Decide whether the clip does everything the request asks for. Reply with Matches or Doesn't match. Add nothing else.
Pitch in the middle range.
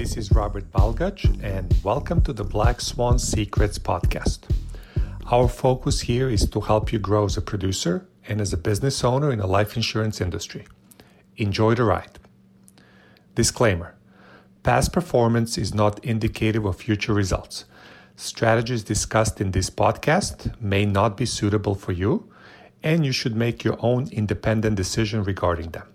Doesn't match